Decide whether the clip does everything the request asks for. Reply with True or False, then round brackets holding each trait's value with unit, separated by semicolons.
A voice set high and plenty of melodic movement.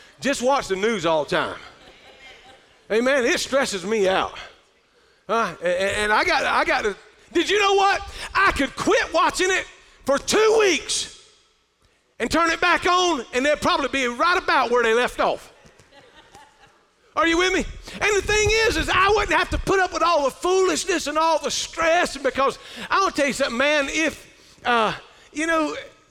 True (325 Hz; 5.8 semitones)